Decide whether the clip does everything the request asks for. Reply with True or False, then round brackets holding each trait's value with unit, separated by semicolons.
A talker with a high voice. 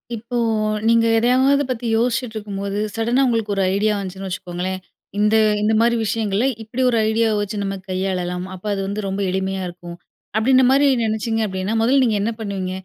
True (215 Hz)